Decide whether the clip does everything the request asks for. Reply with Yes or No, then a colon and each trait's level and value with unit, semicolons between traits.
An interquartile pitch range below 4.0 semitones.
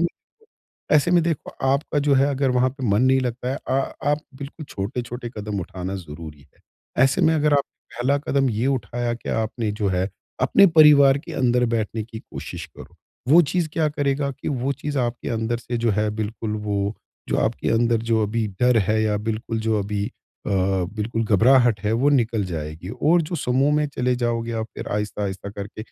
No: average, 4.5 semitones